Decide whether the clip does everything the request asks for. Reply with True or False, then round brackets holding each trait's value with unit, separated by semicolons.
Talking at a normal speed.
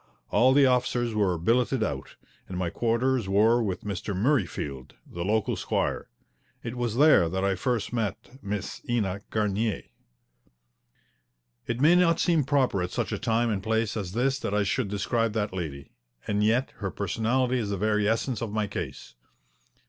True (170 wpm)